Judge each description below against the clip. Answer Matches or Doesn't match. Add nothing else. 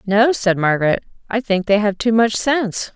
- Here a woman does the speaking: Matches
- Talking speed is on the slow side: Doesn't match